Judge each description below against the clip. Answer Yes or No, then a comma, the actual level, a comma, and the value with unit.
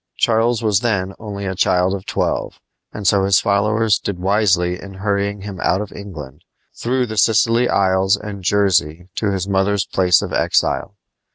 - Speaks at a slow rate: No, average, 170 wpm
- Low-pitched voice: Yes, low, 100 Hz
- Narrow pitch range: Yes, narrow, 2.0 semitones